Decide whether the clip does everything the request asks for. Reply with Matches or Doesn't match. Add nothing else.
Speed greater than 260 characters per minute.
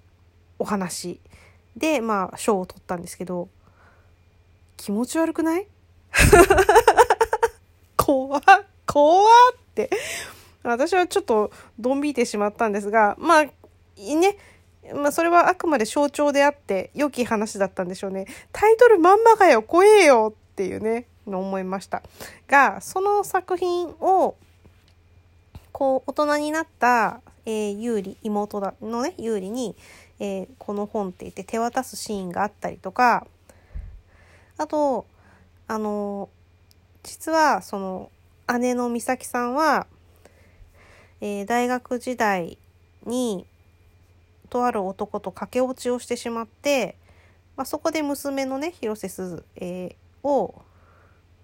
Doesn't match